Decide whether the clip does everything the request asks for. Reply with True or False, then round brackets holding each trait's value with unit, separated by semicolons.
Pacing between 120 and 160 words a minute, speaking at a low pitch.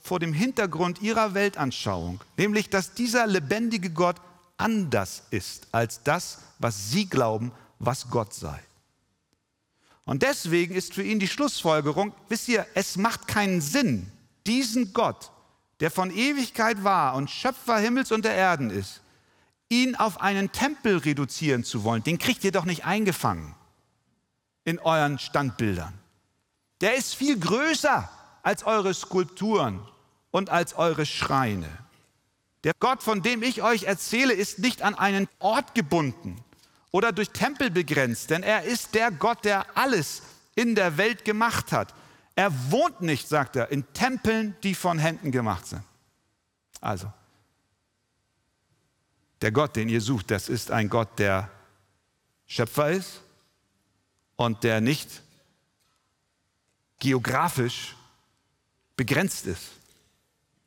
False (130 wpm; 160 Hz)